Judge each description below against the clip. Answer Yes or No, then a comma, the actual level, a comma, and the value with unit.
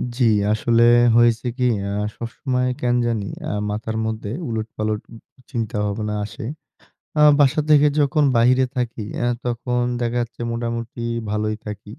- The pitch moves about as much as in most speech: No, narrow, 2.1 semitones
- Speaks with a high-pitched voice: No, low, 115 Hz